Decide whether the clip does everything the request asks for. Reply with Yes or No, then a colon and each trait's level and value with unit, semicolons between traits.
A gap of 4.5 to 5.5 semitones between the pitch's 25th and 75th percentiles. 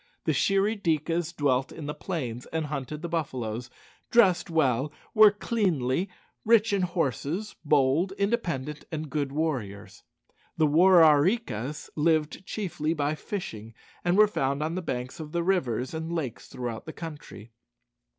Yes: average, 4.9 semitones